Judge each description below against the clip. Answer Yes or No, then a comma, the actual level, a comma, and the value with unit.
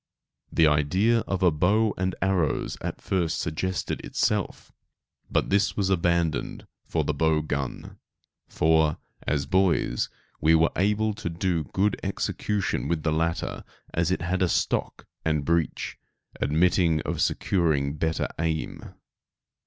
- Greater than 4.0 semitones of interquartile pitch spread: No, average, 3.2 semitones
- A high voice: No, very low, 85 Hz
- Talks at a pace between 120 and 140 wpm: Yes, slow, 135 wpm